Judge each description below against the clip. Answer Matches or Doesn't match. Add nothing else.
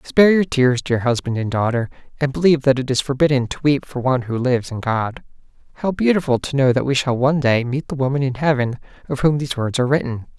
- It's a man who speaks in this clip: Matches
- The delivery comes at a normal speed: Doesn't match